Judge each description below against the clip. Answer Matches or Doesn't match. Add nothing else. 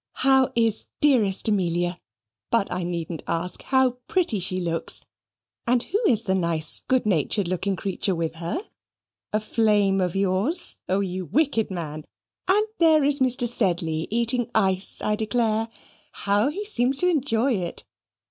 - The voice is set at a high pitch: Matches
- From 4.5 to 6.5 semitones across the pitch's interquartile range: Matches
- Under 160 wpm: Matches